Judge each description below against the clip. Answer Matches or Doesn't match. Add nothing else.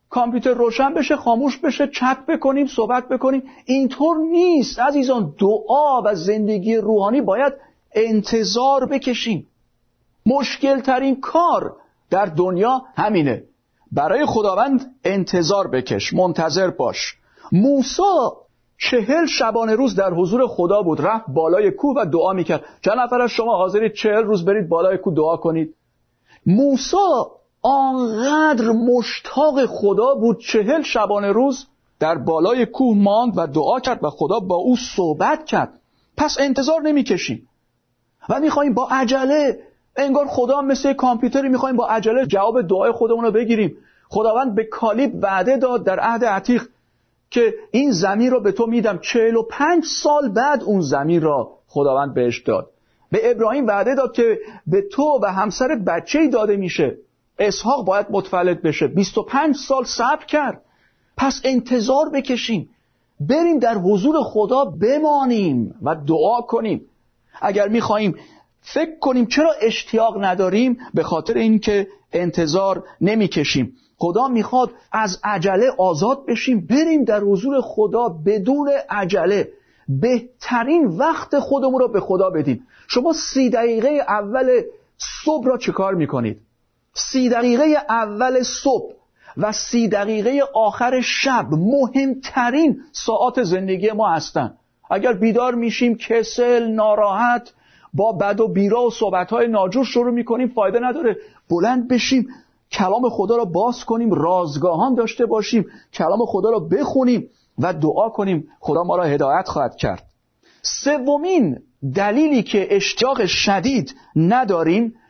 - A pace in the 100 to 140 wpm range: Matches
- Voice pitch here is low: Doesn't match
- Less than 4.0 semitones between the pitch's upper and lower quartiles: Doesn't match